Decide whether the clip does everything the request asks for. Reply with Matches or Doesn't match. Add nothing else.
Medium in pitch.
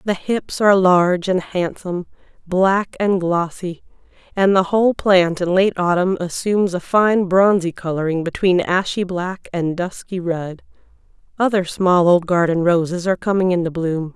Matches